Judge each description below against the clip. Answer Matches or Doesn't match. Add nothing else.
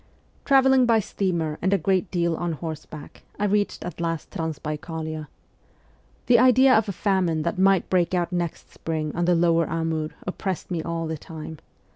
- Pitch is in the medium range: Matches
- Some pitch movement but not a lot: Matches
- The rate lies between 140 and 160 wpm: Doesn't match